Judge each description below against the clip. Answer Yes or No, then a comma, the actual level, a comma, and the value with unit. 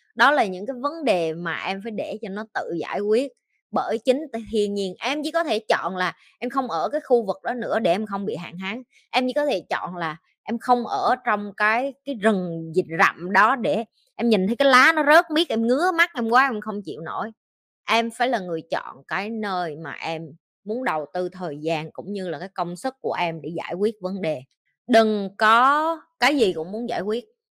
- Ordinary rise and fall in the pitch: No, wide, 6.0 semitones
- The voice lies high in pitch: Yes, high, 215 Hz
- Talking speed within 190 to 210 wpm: No, average, 235 wpm